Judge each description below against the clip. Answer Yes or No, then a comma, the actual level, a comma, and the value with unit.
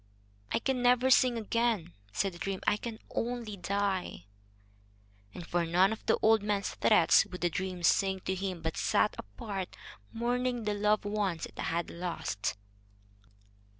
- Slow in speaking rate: No, average, 155 wpm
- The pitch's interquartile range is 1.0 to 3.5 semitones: No, average, 4.1 semitones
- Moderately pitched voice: No, high, 200 Hz